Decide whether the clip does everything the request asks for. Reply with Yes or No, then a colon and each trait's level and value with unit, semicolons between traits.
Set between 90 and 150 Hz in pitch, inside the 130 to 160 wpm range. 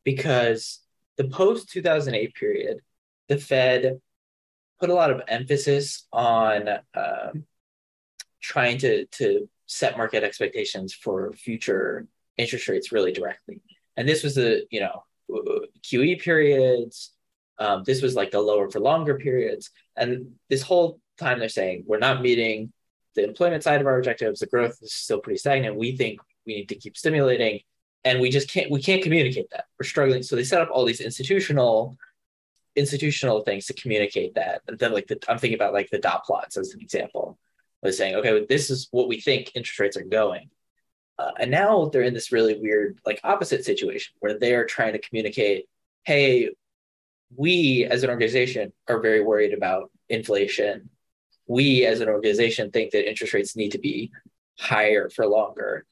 No: medium, 140 Hz; average, 170 wpm